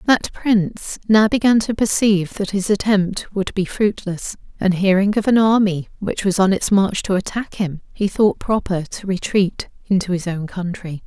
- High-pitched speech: Yes, high, 195 Hz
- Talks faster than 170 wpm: Yes, average, 185 wpm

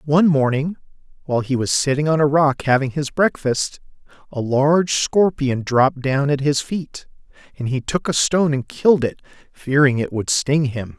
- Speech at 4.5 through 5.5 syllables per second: Yes, 5.0 syllables/s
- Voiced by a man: Yes, male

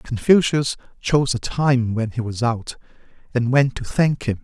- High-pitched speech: No, low, 125 Hz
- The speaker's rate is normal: Yes, average, 175 wpm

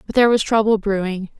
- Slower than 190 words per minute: No, fast, 215 wpm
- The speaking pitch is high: Yes, high, 210 Hz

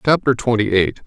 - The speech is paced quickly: No, average, 170 wpm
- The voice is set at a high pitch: No, low, 120 Hz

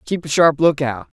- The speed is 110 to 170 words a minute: No, average, 200 wpm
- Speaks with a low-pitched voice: No, medium, 150 Hz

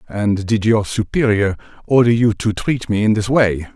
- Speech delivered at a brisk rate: No, average, 190 wpm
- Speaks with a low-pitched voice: Yes, low, 110 Hz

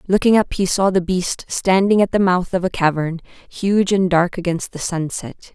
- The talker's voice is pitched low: No, medium, 185 Hz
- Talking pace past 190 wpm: Yes, fast, 205 wpm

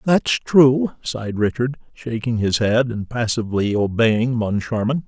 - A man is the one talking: Yes, male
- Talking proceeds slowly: Yes, slow, 130 wpm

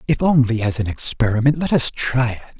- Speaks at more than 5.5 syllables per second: Yes, 5.7 syllables/s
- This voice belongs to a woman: No, male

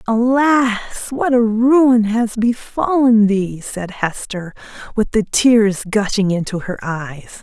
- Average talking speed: No, slow, 130 wpm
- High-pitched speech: Yes, high, 220 Hz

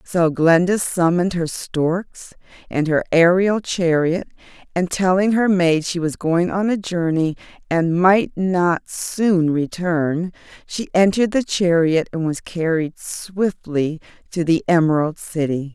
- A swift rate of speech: No, slow, 135 wpm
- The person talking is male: No, female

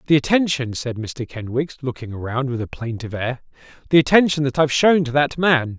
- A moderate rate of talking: Yes, average, 195 wpm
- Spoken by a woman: No, male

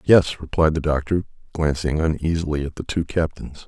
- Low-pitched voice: Yes, very low, 80 Hz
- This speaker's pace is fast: No, average, 165 wpm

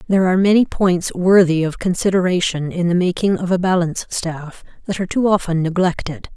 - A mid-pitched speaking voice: Yes, medium, 180 Hz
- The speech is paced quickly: No, average, 180 wpm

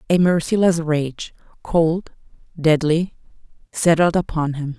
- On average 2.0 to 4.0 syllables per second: Yes, 3.9 syllables/s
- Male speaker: No, female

